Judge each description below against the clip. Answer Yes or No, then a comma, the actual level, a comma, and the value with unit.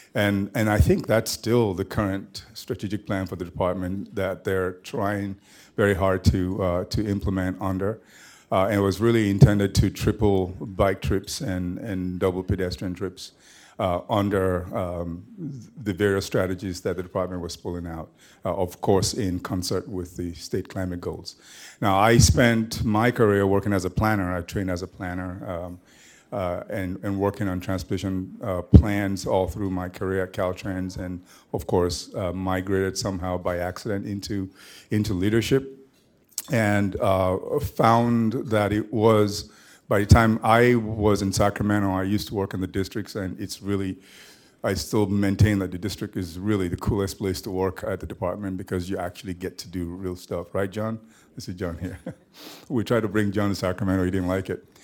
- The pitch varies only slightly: Yes, narrow, 2.1 semitones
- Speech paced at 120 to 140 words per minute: No, average, 180 wpm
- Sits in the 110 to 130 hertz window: No, very low, 95 Hz